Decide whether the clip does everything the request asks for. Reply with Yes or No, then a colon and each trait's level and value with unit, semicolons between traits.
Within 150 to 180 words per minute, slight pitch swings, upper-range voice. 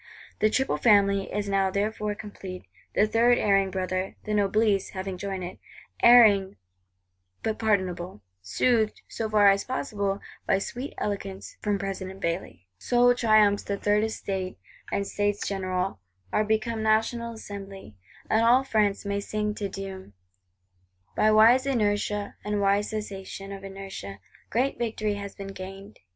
No: average, 140 wpm; narrow, 1.9 semitones; high, 205 Hz